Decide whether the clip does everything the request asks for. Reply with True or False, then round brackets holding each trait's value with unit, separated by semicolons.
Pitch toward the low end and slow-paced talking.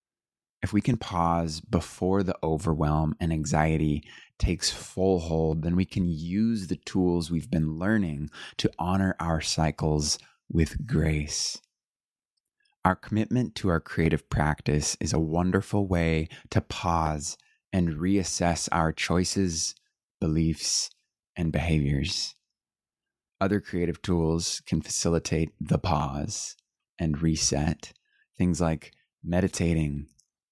True (85 Hz; 115 wpm)